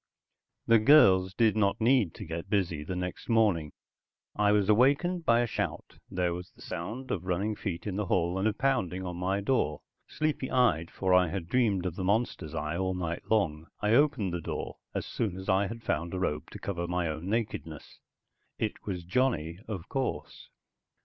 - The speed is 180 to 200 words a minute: Yes, average, 195 wpm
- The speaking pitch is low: Yes, very low, 95 Hz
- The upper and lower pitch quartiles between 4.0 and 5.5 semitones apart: Yes, average, 4.3 semitones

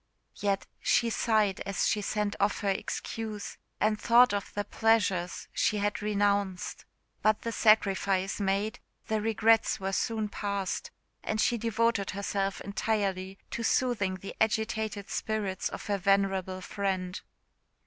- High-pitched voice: Yes, high, 205 Hz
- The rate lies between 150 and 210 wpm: No, slow, 135 wpm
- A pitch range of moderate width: No, narrow, 2.0 semitones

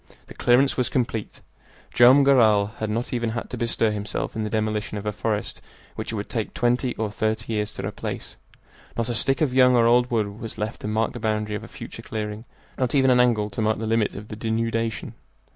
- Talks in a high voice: No, low, 110 Hz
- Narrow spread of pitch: Yes, narrow, 2.3 semitones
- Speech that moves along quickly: Yes, fast, 225 wpm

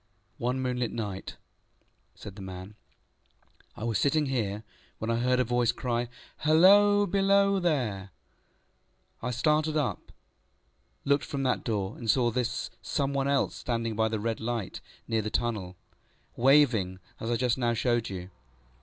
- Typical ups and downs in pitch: Yes, average, 4.1 semitones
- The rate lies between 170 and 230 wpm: No, average, 155 wpm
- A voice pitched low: Yes, low, 120 Hz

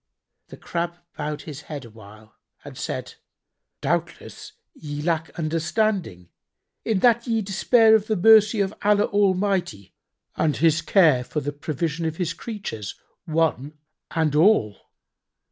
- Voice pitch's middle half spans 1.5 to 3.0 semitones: No, wide, 5.6 semitones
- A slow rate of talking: Yes, slow, 130 wpm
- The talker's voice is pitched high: No, medium, 165 Hz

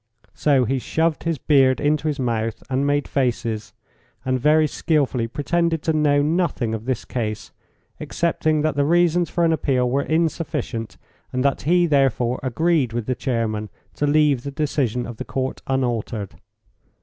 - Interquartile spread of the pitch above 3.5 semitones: Yes, average, 4.2 semitones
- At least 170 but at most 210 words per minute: No, average, 160 wpm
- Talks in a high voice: No, medium, 140 Hz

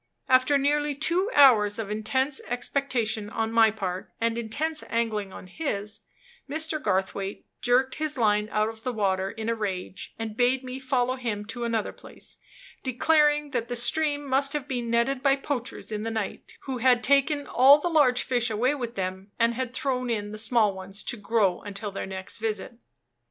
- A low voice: No, high, 235 Hz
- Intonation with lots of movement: No, average, 4.2 semitones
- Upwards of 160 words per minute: Yes, average, 185 wpm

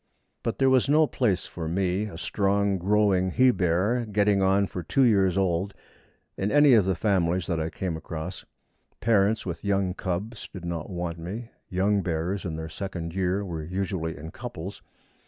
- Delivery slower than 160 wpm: No, average, 175 wpm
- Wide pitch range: No, average, 3.0 semitones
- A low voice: Yes, very low, 95 Hz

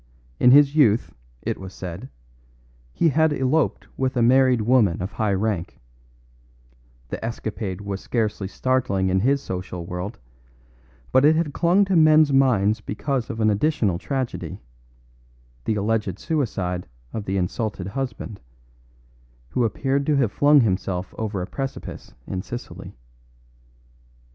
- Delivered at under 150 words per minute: Yes, slow, 135 wpm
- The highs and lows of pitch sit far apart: Yes, wide, 5.8 semitones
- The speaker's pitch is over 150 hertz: No, low, 115 Hz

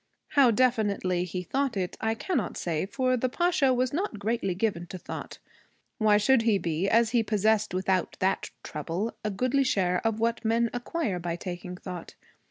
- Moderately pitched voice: No, high, 215 Hz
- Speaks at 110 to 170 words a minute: No, average, 180 wpm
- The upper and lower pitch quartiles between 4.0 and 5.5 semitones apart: Yes, average, 5.0 semitones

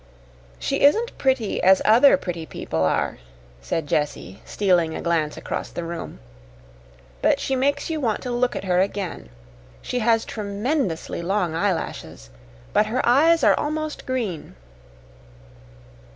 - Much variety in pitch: Yes, wide, 7.4 semitones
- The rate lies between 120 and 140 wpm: Yes, slow, 135 wpm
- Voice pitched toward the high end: Yes, high, 205 Hz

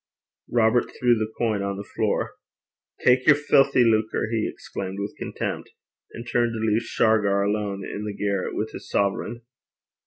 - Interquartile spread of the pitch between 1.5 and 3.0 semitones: Yes, average, 2.7 semitones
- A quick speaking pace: No, average, 160 wpm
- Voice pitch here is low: Yes, low, 110 Hz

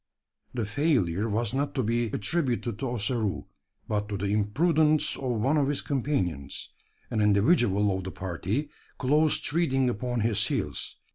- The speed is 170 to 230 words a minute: No, average, 150 wpm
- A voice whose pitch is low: Yes, low, 120 Hz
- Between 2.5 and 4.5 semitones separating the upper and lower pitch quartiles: No, average, 5.2 semitones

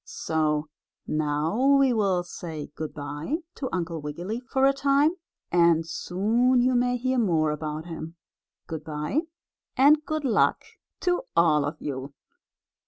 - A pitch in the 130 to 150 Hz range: No, medium, 175 Hz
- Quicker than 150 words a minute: No, average, 140 wpm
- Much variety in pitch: Yes, wide, 8.8 semitones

